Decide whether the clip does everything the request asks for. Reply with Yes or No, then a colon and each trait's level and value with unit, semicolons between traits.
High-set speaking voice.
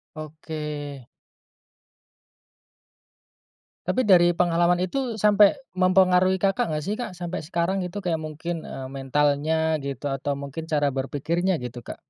No: medium, 165 Hz